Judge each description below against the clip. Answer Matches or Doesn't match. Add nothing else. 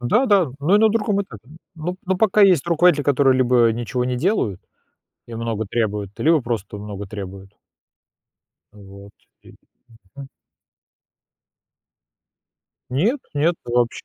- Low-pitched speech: Matches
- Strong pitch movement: Matches